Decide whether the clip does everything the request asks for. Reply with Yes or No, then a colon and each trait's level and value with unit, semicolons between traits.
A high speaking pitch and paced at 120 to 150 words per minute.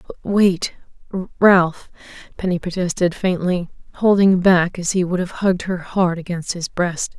No: medium, 180 Hz; average, 140 wpm